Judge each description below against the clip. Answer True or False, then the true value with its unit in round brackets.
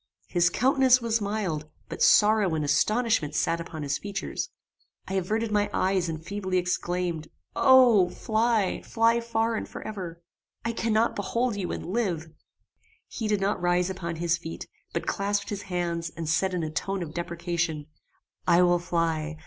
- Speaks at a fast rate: False (165 wpm)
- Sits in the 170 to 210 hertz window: True (185 Hz)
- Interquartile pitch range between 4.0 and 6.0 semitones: True (4.4 semitones)